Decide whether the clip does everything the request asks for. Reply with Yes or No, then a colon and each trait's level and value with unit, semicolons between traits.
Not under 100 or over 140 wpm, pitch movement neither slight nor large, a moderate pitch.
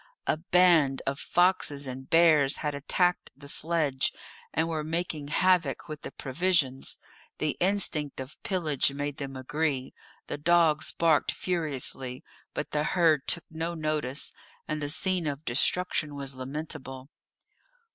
Yes: slow, 135 wpm; average, 3.3 semitones; medium, 150 Hz